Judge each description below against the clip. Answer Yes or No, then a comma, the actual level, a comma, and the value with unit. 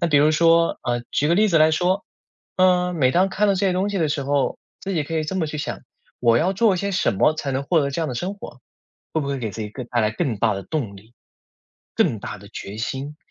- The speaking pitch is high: No, medium, 155 Hz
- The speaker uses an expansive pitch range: Yes, wide, 6.0 semitones